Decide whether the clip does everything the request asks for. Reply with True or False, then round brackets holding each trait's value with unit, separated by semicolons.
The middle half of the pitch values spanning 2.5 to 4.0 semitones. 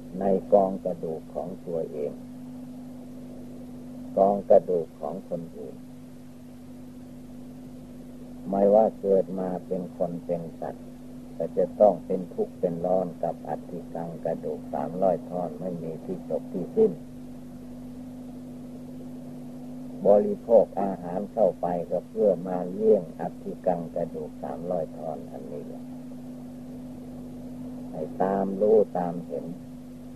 False (4.5 semitones)